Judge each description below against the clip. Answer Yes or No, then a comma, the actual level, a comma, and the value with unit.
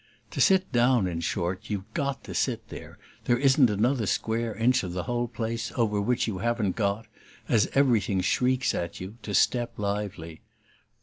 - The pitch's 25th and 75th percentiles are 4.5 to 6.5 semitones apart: No, average, 3.6 semitones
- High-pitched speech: No, low, 110 Hz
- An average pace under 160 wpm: No, average, 175 wpm